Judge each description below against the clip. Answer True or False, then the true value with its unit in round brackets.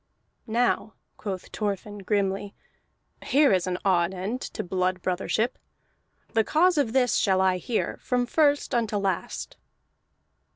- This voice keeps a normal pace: False (130 wpm)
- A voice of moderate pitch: False (205 Hz)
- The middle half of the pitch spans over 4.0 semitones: True (4.6 semitones)